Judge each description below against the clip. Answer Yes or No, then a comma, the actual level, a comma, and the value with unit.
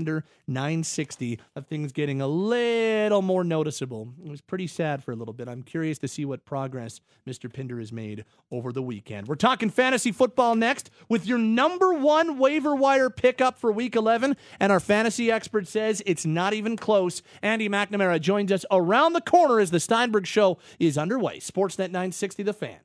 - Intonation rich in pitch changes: Yes, wide, 7.6 semitones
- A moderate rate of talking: Yes, average, 185 wpm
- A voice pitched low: No, high, 190 Hz